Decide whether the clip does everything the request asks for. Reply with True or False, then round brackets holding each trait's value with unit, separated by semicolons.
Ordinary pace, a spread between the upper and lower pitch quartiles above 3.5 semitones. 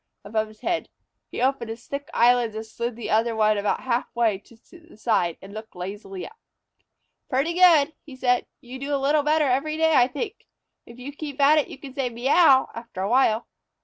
False (210 wpm; 4.5 semitones)